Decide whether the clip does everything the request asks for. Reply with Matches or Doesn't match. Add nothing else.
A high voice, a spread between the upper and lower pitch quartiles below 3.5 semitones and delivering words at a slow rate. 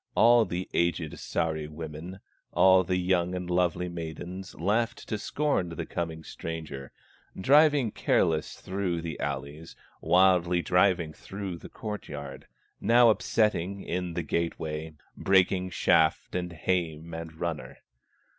Doesn't match